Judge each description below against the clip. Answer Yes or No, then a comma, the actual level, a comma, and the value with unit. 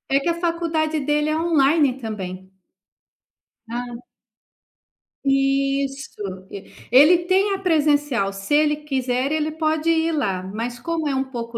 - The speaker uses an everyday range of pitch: Yes, average, 4.3 semitones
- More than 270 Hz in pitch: Yes, very high, 290 Hz